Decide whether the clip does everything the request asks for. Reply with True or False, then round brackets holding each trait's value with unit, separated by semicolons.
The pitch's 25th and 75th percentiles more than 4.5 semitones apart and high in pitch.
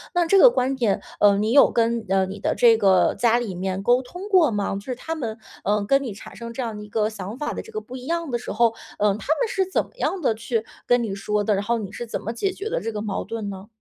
False (4.1 semitones; 230 Hz)